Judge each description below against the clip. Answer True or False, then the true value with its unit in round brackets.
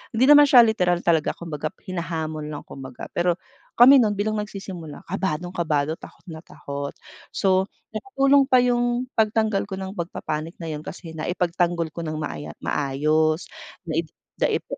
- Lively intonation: False (5.0 semitones)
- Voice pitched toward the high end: False (175 Hz)